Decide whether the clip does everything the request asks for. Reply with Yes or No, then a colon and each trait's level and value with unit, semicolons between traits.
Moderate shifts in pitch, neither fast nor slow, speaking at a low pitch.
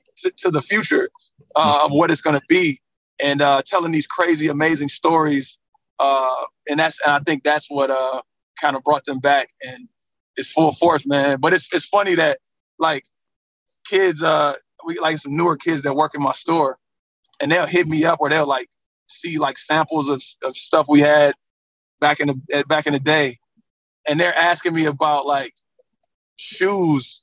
No: average, 3.3 semitones; average, 185 wpm; medium, 150 Hz